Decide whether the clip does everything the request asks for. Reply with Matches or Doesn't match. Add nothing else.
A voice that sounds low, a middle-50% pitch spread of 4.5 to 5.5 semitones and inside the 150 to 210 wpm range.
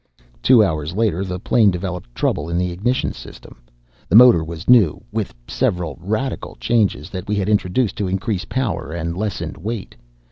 Doesn't match